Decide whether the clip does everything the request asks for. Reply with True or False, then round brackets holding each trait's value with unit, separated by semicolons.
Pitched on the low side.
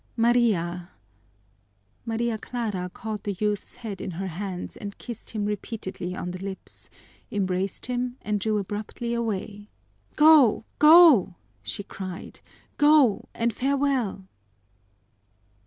False (210 Hz)